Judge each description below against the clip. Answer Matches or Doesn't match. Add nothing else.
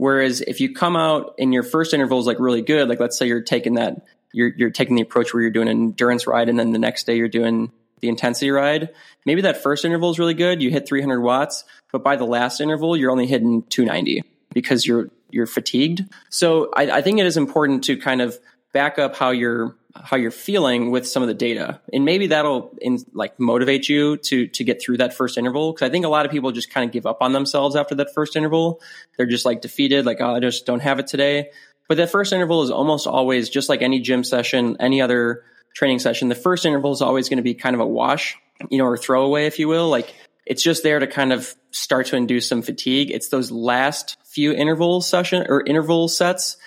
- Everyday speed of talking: Doesn't match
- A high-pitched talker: Doesn't match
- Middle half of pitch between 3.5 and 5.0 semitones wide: Matches